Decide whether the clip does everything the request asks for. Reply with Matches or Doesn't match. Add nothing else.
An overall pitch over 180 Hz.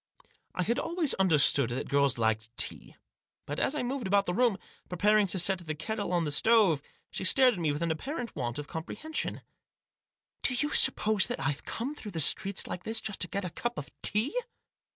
Matches